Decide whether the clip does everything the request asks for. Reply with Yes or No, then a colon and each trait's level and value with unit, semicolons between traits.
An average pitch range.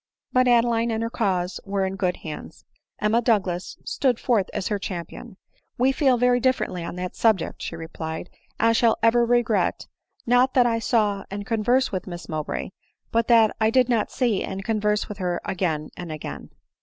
Yes: average, 4.4 semitones